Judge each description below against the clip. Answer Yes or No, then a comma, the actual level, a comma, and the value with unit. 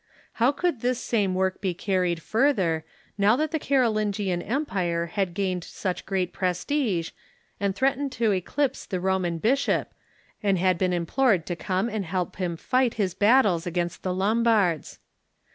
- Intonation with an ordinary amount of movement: Yes, average, 4.6 semitones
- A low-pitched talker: No, high, 195 Hz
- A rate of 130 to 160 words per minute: Yes, average, 155 wpm